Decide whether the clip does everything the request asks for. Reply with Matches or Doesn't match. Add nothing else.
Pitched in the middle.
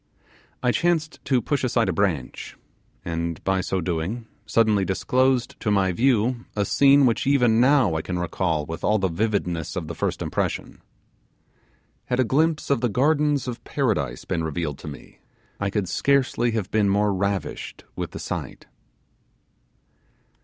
Doesn't match